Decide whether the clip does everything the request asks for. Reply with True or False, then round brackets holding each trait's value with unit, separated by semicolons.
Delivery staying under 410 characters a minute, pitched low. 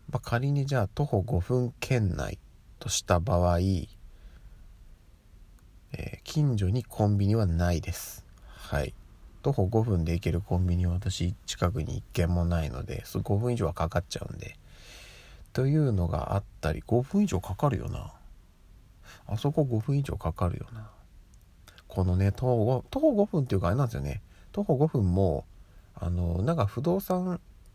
True (275 characters per minute; 95 Hz)